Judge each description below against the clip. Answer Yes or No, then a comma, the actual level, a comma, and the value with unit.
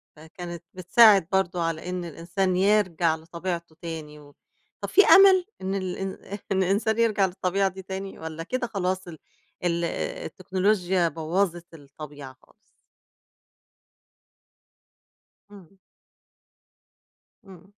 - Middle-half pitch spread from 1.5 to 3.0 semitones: Yes, average, 2.7 semitones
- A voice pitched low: No, medium, 180 Hz